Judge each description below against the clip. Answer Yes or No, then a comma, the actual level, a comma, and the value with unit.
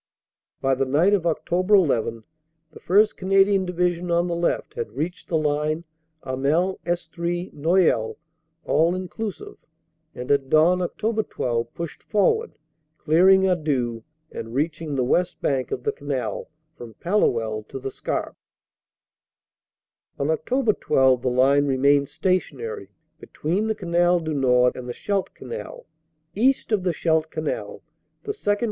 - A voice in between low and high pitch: Yes, medium, 165 Hz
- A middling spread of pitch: No, wide, 5.7 semitones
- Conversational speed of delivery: Yes, average, 145 wpm